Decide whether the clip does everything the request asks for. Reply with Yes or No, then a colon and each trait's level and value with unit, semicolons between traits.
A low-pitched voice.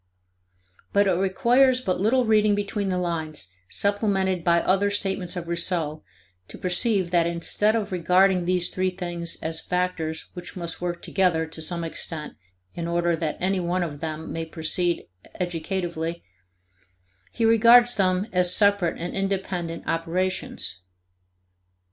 No: medium, 180 Hz